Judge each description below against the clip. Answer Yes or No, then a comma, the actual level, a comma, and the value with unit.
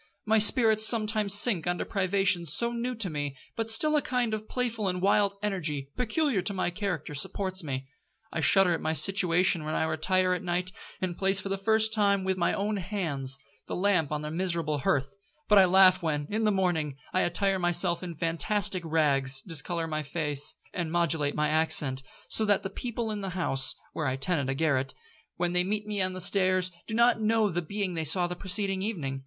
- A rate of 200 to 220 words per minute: Yes, fast, 205 wpm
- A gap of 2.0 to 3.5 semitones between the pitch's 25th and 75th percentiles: No, average, 4.4 semitones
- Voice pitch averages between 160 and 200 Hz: Yes, medium, 185 Hz